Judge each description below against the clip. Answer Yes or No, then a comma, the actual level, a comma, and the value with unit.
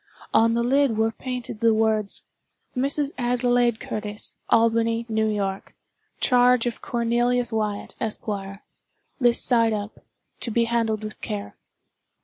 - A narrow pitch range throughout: Yes, narrow, 1.9 semitones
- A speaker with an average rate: No, slow, 125 wpm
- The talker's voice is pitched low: No, high, 230 Hz